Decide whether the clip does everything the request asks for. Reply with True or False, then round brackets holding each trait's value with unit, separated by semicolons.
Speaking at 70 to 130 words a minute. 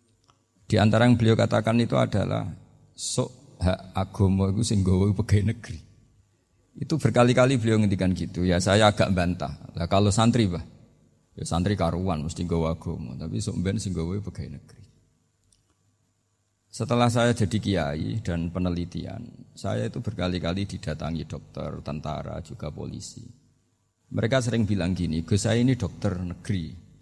False (140 wpm)